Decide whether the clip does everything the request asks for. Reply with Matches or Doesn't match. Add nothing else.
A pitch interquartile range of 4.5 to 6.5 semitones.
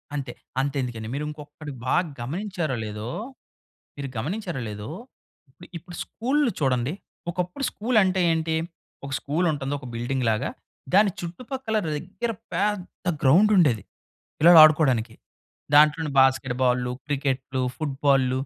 Matches